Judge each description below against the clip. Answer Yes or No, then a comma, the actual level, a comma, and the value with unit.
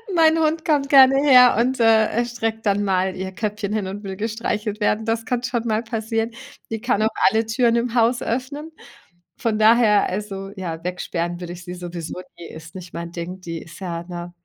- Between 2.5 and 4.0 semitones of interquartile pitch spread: No, average, 4.4 semitones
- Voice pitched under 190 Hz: No, high, 215 Hz